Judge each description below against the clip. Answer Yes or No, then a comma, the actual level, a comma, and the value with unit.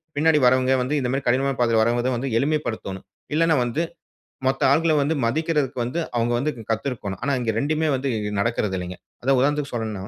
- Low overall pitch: Yes, low, 130 Hz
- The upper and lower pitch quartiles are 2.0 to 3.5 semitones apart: No, average, 4.0 semitones